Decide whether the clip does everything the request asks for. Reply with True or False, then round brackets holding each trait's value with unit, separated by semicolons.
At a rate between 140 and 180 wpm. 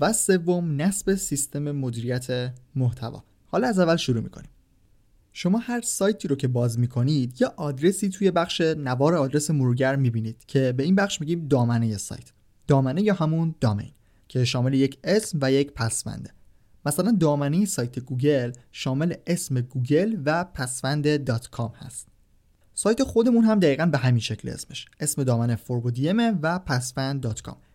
True (150 wpm)